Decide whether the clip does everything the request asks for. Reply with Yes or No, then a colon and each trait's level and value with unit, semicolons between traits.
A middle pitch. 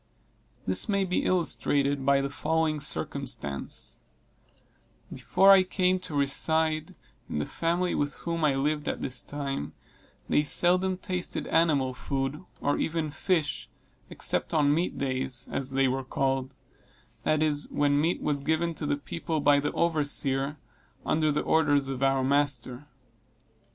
Yes: medium, 145 Hz